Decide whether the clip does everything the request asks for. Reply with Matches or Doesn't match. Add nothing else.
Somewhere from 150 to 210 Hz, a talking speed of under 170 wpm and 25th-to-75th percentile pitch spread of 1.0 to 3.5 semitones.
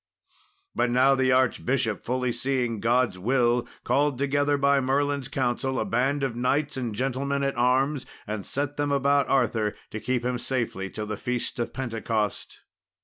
Doesn't match